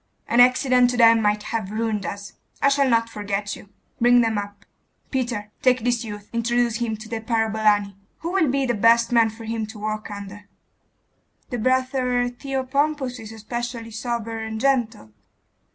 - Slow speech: No, average, 170 wpm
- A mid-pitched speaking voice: No, high, 230 Hz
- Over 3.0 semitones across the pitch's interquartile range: No, narrow, 2.5 semitones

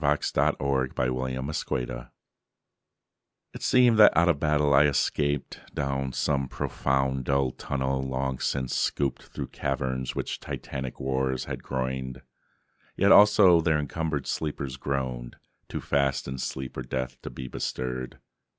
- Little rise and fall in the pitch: Yes, narrow, 1.9 semitones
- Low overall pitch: Yes, very low, 65 Hz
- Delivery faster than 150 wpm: No, slow, 135 wpm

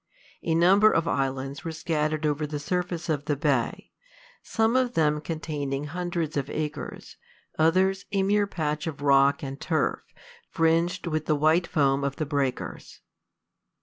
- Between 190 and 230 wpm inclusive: No, average, 150 wpm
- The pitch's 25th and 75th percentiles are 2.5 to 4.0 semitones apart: Yes, average, 3.2 semitones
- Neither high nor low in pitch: Yes, medium, 155 Hz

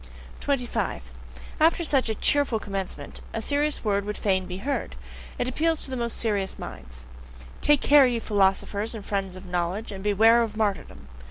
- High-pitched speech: Yes, high, 215 Hz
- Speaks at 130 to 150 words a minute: No, average, 170 wpm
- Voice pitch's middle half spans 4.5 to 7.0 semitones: Yes, average, 4.9 semitones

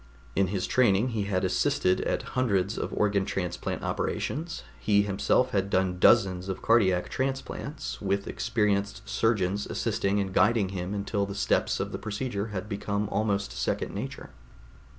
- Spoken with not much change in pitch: Yes, narrow, 2.3 semitones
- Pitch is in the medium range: No, low, 100 Hz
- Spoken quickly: No, average, 150 wpm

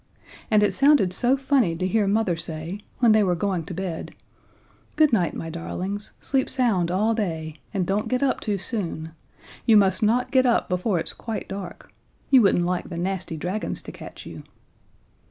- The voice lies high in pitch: Yes, high, 195 Hz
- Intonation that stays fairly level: No, average, 4.3 semitones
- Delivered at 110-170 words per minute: No, average, 185 wpm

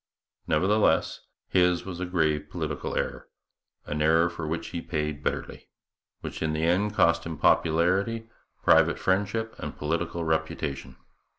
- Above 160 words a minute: No, slow, 135 wpm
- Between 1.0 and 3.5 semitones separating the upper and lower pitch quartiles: Yes, average, 2.9 semitones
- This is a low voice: Yes, very low, 85 Hz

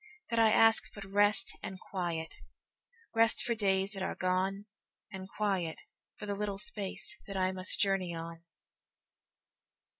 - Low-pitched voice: No, high, 195 Hz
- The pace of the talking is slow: Yes, slow, 125 wpm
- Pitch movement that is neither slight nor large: No, narrow, 1.9 semitones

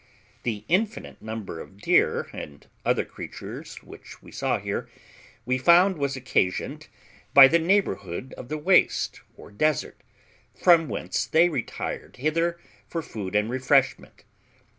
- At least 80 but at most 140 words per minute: Yes, slow, 135 wpm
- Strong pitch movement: Yes, wide, 7.6 semitones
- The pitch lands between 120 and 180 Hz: Yes, medium, 140 Hz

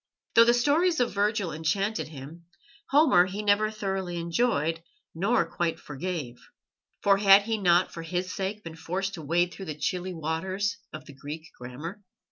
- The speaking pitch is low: No, medium, 185 Hz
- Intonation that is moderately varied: Yes, average, 3.8 semitones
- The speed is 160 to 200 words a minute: Yes, average, 165 wpm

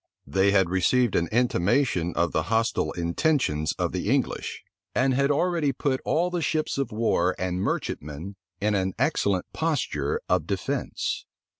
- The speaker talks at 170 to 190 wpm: No, average, 150 wpm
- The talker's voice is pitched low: Yes, low, 105 Hz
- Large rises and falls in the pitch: Yes, wide, 7.6 semitones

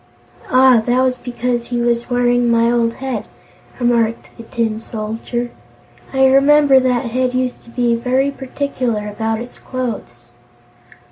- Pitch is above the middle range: Yes, high, 245 Hz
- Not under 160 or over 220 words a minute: No, average, 140 wpm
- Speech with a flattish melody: Yes, narrow, 1.7 semitones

